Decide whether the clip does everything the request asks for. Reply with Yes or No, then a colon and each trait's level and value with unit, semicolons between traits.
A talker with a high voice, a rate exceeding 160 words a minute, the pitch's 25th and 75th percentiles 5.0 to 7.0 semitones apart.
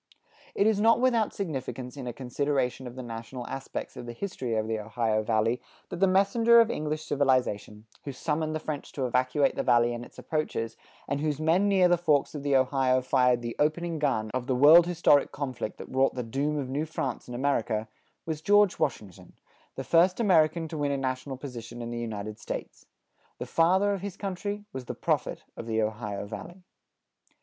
No: low, 135 Hz; average, 195 wpm; wide, 5.5 semitones